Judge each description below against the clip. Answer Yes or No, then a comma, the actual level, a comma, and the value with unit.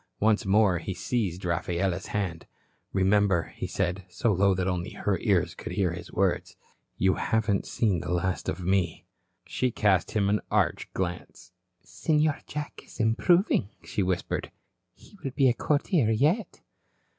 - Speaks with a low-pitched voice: Yes, low, 100 Hz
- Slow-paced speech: No, average, 155 wpm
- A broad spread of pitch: No, average, 3.7 semitones